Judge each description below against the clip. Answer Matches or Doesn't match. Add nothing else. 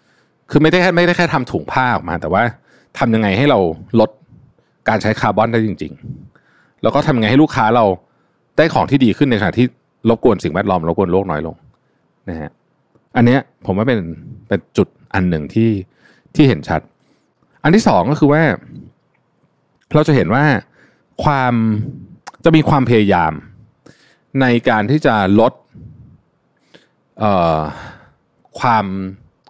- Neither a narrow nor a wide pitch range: Doesn't match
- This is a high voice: Doesn't match